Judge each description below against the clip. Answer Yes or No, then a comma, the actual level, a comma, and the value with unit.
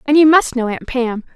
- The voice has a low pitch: No, very high, 265 Hz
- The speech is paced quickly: Yes, fast, 265 wpm